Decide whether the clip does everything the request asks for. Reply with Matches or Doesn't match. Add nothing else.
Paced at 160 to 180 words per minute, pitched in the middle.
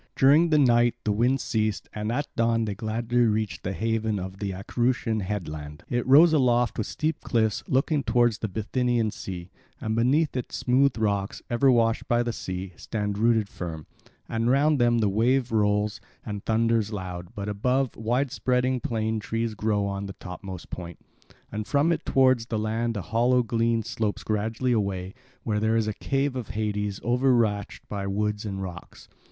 Doesn't match